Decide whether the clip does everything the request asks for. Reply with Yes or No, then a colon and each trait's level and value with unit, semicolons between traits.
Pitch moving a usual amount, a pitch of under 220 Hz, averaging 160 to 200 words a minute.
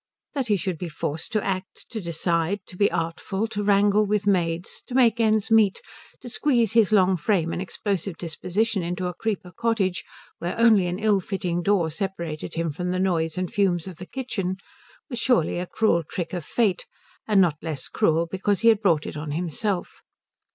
Yes: average, 3.7 semitones; high, 190 Hz; average, 195 wpm